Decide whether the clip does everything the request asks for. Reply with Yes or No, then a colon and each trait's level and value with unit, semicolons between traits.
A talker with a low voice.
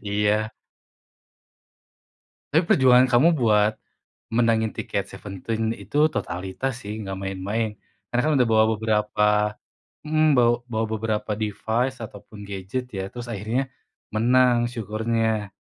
Yes: low, 110 Hz